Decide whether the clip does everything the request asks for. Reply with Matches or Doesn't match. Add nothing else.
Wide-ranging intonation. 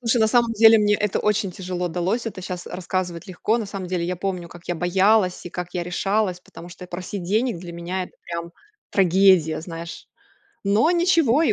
Doesn't match